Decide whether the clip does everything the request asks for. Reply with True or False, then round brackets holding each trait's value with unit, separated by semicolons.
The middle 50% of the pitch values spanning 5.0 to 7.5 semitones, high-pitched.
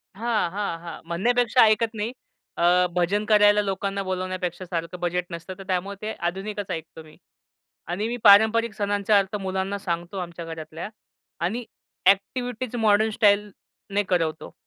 False (3.2 semitones; 195 Hz)